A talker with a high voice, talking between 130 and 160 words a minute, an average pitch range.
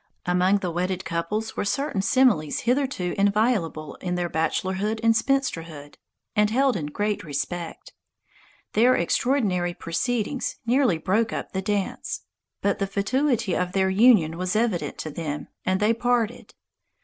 Yes: high, 195 Hz; average, 140 wpm; average, 4.7 semitones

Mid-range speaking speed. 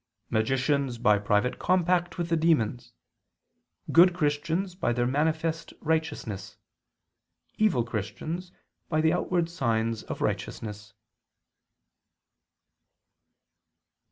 No: slow, 90 wpm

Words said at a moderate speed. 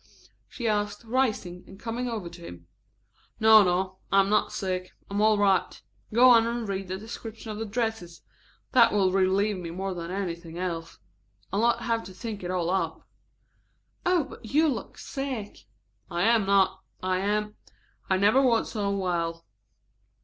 Yes: average, 170 wpm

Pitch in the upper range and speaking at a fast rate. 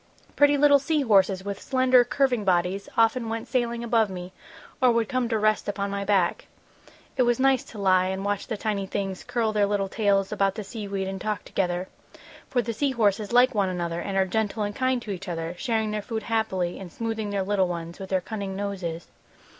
Yes: high, 205 Hz; fast, 215 wpm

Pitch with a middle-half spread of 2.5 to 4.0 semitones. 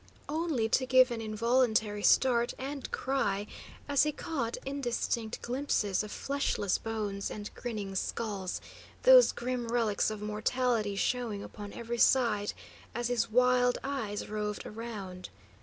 Yes: average, 3.4 semitones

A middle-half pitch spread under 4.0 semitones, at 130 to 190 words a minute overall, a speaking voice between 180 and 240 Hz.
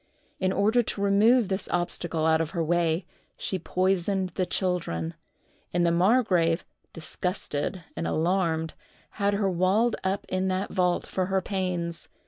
Yes: narrow, 2.4 semitones; average, 145 wpm; medium, 185 Hz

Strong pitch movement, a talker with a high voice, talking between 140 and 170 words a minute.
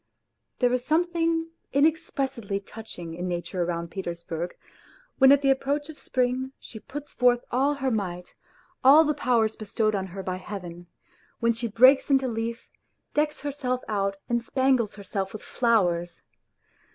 Yes: wide, 5.9 semitones; high, 235 Hz; average, 150 wpm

